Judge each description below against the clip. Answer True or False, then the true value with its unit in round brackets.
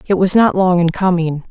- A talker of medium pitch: True (180 Hz)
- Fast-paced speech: True (240 wpm)